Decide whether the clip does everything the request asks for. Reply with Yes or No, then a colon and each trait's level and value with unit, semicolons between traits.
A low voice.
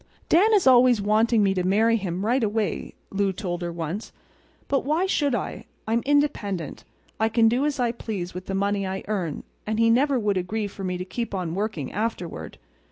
No: high, 210 Hz